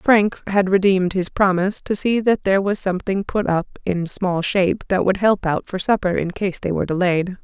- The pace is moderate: No, fast, 220 wpm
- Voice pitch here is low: No, high, 190 Hz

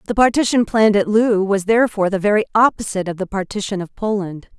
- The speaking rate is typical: Yes, average, 195 wpm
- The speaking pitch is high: Yes, high, 205 Hz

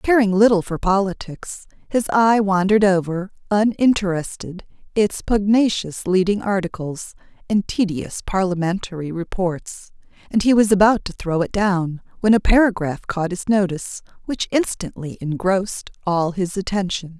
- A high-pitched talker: Yes, high, 195 Hz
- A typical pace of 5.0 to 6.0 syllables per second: No, 4.7 syllables/s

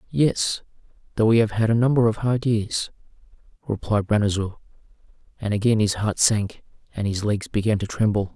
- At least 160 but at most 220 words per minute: Yes, average, 165 wpm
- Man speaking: Yes, male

